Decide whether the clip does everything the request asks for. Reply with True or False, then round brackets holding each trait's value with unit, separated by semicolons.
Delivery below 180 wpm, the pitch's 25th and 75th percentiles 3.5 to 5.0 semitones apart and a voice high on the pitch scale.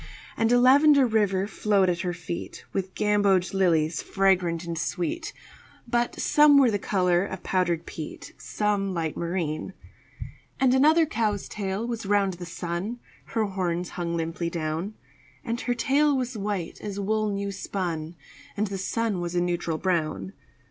True (155 wpm; 3.9 semitones; 195 Hz)